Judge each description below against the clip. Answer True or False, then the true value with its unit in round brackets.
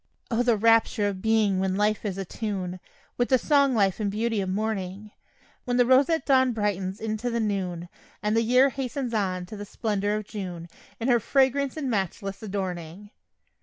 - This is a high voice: True (215 Hz)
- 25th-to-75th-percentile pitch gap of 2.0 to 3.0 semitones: False (3.8 semitones)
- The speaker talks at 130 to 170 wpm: False (185 wpm)